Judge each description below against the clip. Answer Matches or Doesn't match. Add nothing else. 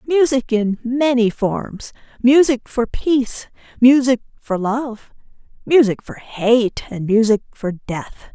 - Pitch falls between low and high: Doesn't match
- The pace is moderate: Doesn't match